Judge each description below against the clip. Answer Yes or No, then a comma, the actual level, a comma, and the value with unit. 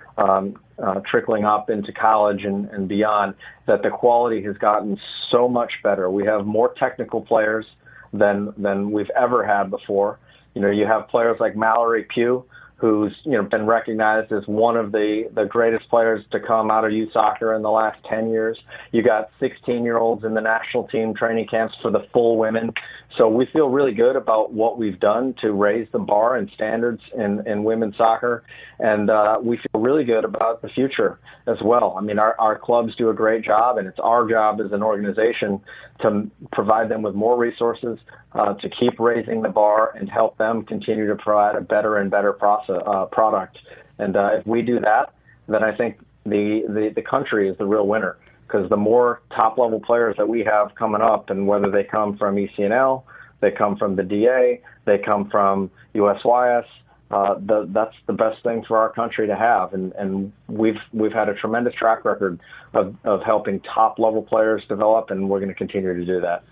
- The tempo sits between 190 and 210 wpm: Yes, average, 200 wpm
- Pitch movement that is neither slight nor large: No, narrow, 1.8 semitones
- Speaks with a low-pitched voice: Yes, low, 110 Hz